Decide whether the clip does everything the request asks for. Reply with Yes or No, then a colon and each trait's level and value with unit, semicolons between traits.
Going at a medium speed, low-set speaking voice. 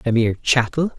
Yes: average, 185 wpm; low, 125 Hz